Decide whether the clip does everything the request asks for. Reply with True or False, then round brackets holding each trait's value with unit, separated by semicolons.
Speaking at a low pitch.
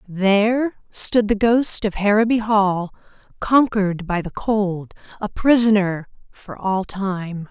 False (205 Hz)